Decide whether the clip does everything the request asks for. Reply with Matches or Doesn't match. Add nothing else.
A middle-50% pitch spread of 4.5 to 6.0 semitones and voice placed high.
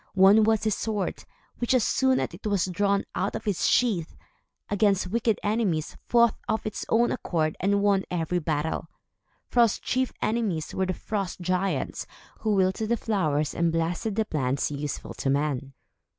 Matches